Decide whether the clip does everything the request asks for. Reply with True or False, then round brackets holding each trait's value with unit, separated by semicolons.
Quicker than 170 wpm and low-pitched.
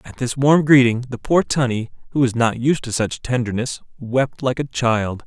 True (205 wpm; 125 Hz)